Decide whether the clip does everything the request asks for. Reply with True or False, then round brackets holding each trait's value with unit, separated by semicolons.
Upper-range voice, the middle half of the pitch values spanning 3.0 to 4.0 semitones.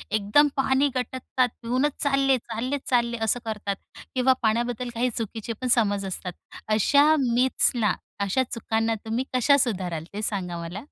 True (235 Hz; 3.6 semitones)